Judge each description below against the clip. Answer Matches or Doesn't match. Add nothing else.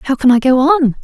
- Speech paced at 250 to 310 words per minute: Matches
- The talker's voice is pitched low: Doesn't match